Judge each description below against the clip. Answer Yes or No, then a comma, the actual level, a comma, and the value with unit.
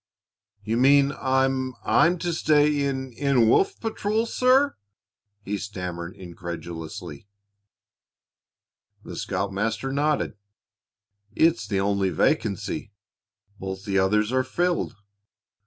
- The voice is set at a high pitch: No, low, 115 Hz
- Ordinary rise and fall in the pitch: No, wide, 7.3 semitones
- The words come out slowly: Yes, slow, 100 wpm